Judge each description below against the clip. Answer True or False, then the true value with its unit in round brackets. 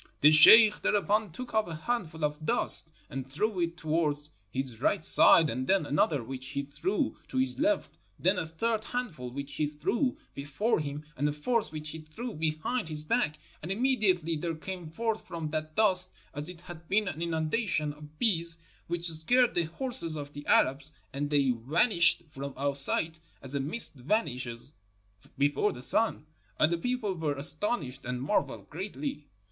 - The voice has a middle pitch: True (160 Hz)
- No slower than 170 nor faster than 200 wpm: True (180 wpm)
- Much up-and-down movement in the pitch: True (5.8 semitones)